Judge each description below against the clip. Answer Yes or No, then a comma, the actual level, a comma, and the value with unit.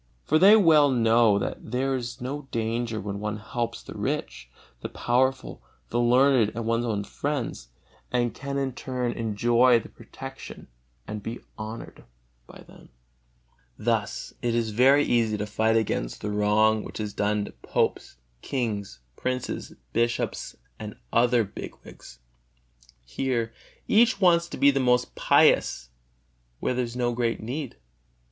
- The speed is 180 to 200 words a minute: No, average, 150 wpm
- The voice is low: Yes, low, 120 Hz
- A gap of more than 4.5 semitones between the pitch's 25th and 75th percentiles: No, average, 3.0 semitones